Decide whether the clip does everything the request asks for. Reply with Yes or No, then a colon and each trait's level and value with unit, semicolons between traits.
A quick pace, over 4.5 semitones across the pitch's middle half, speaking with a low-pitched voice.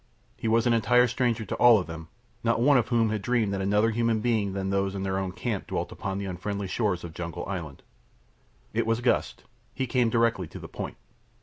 No: fast, 220 wpm; average, 3.3 semitones; low, 110 Hz